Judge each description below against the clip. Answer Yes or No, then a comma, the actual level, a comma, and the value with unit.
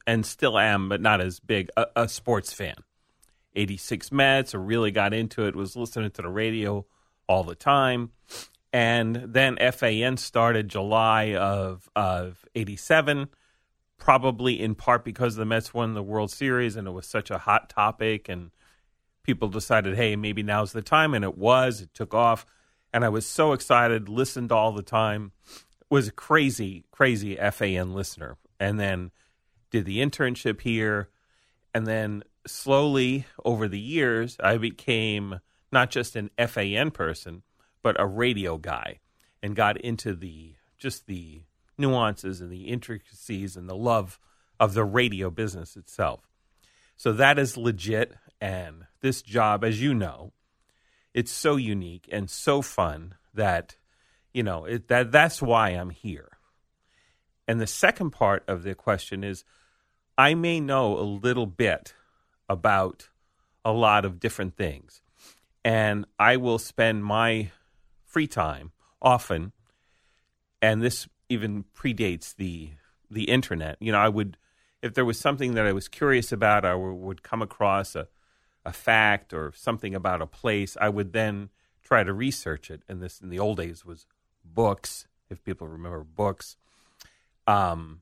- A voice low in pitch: Yes, low, 110 Hz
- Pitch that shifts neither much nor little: Yes, average, 3.8 semitones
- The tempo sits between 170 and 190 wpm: No, average, 155 wpm